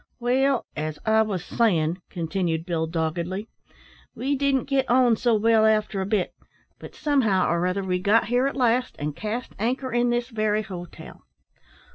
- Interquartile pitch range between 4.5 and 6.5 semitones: Yes, average, 5.2 semitones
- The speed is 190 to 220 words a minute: No, average, 165 wpm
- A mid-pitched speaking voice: No, high, 215 Hz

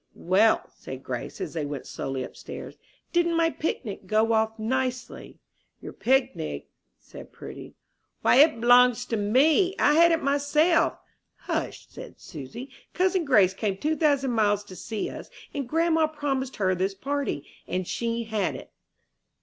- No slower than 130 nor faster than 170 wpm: Yes, average, 150 wpm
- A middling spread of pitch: No, wide, 6.6 semitones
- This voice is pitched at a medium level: No, very high, 250 Hz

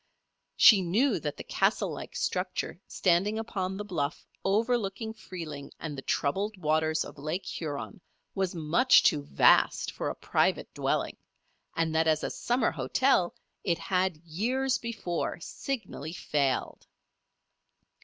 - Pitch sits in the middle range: Yes, medium, 180 Hz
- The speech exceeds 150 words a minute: No, slow, 135 wpm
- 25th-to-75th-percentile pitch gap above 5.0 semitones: Yes, wide, 5.6 semitones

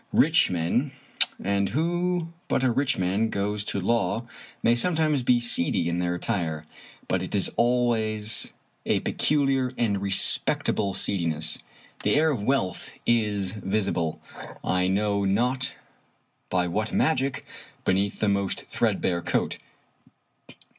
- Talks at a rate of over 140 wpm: No, slow, 135 wpm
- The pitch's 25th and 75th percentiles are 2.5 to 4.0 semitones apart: No, average, 5.0 semitones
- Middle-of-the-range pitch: No, low, 105 Hz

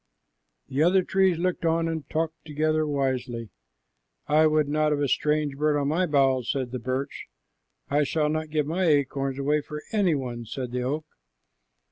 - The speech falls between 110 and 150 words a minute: No, average, 170 wpm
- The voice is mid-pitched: Yes, medium, 150 Hz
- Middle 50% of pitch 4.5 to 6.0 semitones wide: No, narrow, 2.5 semitones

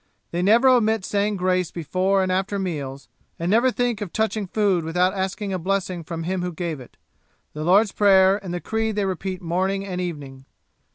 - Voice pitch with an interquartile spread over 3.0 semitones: No, narrow, 2.6 semitones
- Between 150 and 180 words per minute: No, average, 190 wpm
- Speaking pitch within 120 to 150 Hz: No, high, 190 Hz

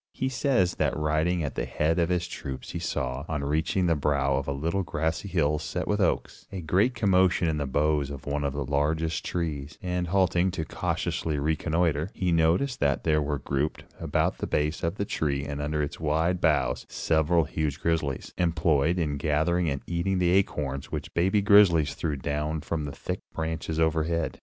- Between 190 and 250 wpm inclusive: Yes, average, 195 wpm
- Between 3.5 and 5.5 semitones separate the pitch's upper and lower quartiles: No, average, 3.1 semitones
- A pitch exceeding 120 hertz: No, very low, 80 Hz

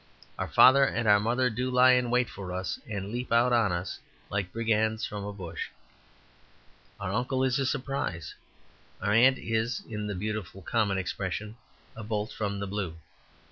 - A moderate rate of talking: Yes, average, 170 wpm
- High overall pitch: No, low, 110 Hz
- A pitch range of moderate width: Yes, average, 3.6 semitones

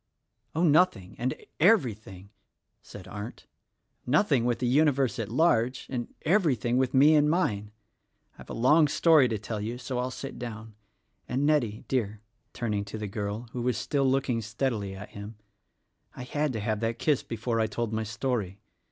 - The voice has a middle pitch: No, low, 120 Hz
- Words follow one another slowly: No, average, 170 wpm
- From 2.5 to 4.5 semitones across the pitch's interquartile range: Yes, average, 4.1 semitones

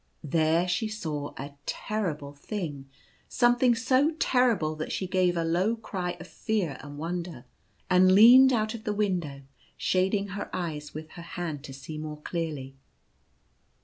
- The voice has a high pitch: No, medium, 175 Hz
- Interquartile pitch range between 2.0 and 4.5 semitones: No, wide, 5.6 semitones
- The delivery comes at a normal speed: Yes, average, 160 wpm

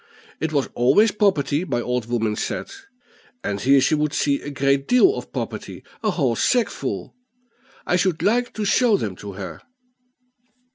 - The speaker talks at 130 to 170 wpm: Yes, average, 160 wpm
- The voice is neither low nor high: Yes, medium, 145 Hz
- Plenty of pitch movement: Yes, wide, 8.4 semitones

